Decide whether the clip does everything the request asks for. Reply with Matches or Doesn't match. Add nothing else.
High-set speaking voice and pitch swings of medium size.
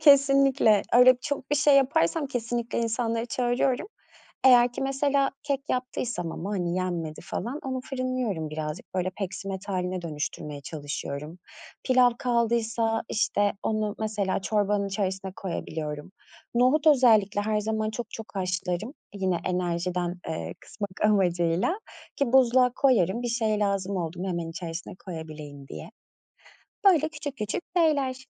Doesn't match